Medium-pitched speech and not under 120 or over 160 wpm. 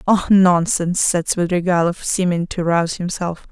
Yes: medium, 175 Hz; slow, 135 wpm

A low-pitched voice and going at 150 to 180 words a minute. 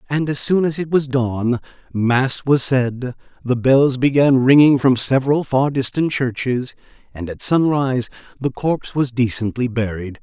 Yes: low, 130 Hz; average, 160 wpm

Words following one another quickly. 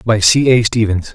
Yes: fast, 210 wpm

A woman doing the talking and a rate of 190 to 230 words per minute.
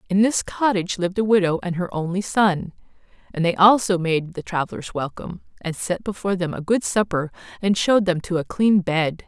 Yes: female; average, 200 wpm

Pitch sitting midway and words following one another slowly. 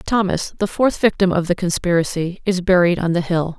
No: medium, 180 Hz; average, 200 wpm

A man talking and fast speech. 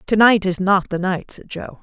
No: female; fast, 265 wpm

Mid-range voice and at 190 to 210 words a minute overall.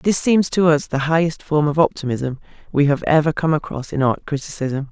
Yes: medium, 150 Hz; fast, 205 wpm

